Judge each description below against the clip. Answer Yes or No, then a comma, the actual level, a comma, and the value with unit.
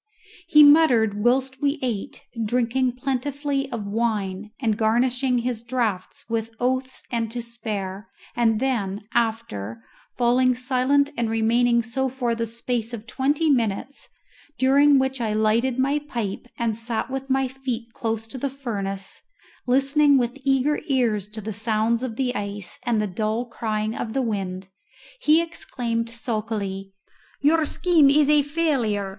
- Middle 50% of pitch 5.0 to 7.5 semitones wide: No, average, 3.4 semitones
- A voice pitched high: Yes, high, 240 Hz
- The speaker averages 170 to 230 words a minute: No, average, 150 wpm